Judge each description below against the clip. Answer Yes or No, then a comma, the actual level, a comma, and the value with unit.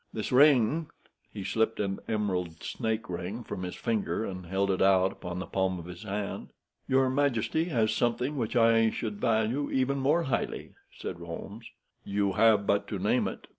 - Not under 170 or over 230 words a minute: Yes, average, 175 wpm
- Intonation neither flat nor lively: Yes, average, 4.2 semitones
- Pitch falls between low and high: No, low, 110 Hz